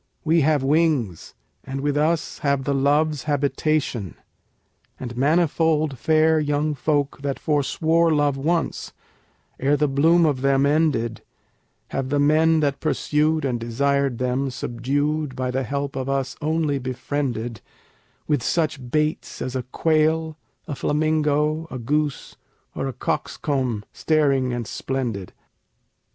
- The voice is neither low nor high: Yes, medium, 145 Hz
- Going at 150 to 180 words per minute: No, slow, 135 wpm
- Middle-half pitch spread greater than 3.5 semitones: No, average, 2.7 semitones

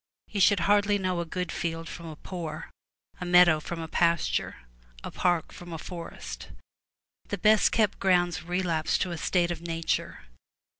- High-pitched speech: No, medium, 175 Hz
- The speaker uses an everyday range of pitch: No, narrow, 1.9 semitones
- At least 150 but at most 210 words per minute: Yes, average, 165 wpm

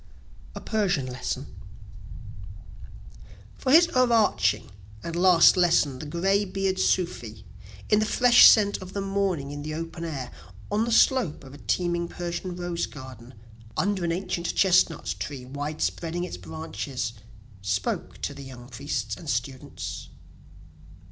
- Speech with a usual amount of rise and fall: No, wide, 6.3 semitones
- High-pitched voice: No, medium, 170 Hz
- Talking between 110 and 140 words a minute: Yes, slow, 135 wpm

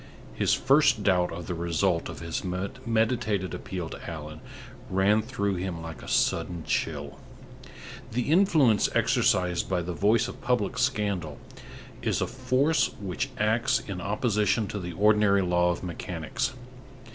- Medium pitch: No, low, 100 Hz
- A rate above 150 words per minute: No, average, 145 wpm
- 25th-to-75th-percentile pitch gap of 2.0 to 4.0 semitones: No, average, 4.7 semitones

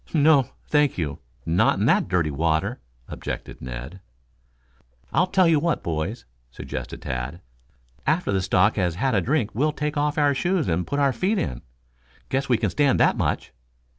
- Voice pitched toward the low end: Yes, low, 120 Hz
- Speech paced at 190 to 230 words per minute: No, average, 170 wpm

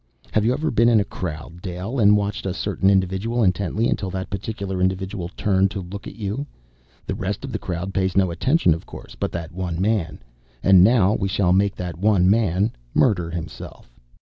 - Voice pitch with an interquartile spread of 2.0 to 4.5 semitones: Yes, narrow, 2.5 semitones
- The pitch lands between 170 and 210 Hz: No, very low, 95 Hz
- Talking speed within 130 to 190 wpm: No, average, 200 wpm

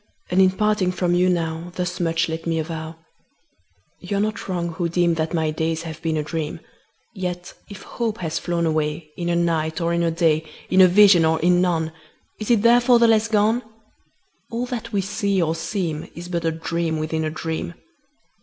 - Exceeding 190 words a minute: Yes, average, 200 wpm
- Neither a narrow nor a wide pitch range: Yes, average, 3.0 semitones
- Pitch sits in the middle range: Yes, medium, 170 Hz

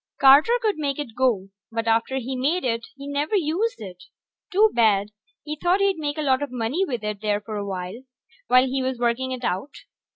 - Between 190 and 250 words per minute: Yes, fast, 205 wpm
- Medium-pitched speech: No, very high, 260 Hz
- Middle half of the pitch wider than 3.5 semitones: Yes, average, 4.9 semitones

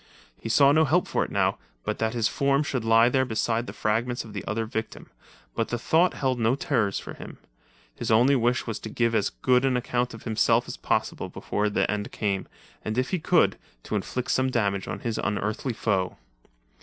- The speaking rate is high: Yes, fast, 215 wpm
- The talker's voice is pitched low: Yes, low, 115 Hz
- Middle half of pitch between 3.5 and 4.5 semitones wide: No, average, 3.0 semitones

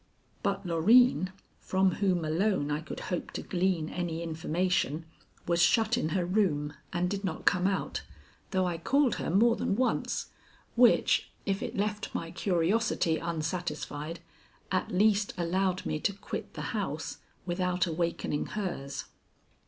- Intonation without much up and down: No, average, 3.2 semitones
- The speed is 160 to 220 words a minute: No, average, 145 wpm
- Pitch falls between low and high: Yes, medium, 180 Hz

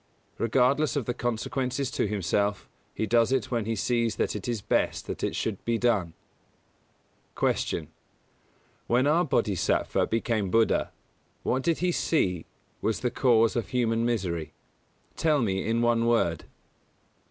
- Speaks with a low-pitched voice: Yes, low, 115 Hz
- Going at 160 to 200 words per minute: No, average, 150 wpm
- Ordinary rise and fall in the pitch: Yes, average, 3.2 semitones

